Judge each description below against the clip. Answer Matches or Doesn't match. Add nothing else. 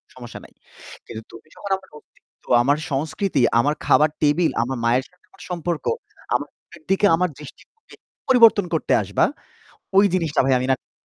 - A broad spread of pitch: Matches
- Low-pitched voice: Doesn't match